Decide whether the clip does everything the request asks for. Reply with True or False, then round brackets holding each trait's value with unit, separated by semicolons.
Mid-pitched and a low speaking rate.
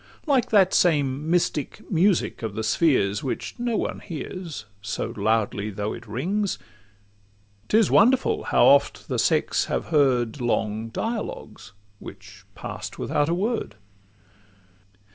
True (145 Hz; 125 wpm)